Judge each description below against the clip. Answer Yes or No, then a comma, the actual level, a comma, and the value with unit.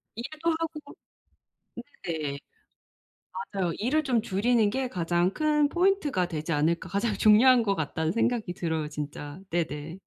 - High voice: Yes, high, 200 Hz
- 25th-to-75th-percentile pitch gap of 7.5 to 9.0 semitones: Yes, wide, 7.8 semitones